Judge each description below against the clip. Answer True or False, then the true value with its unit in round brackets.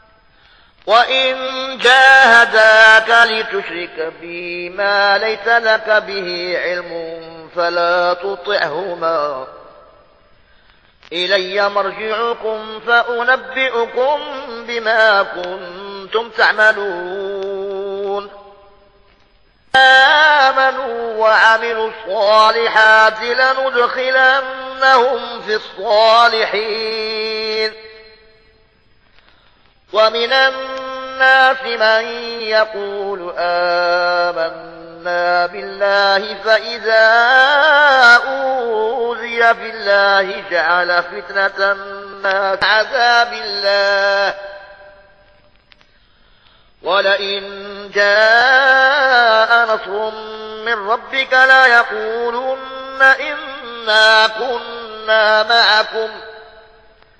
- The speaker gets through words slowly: True (50 wpm)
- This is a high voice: True (220 Hz)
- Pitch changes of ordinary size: True (3.1 semitones)